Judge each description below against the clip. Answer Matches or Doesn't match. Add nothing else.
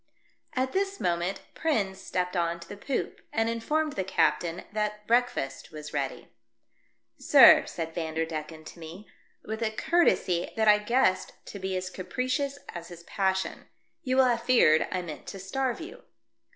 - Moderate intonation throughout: Doesn't match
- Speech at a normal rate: Matches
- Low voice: Doesn't match